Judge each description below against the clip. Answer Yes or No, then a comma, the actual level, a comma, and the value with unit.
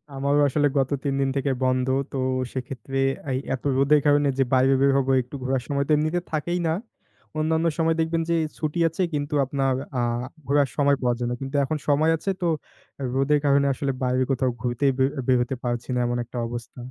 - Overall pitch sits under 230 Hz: Yes, medium, 140 Hz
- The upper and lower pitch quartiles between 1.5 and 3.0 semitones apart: Yes, narrow, 2.4 semitones